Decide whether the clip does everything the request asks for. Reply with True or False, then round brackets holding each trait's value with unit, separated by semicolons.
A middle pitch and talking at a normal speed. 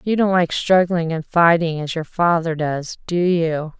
True (170 Hz; 190 wpm)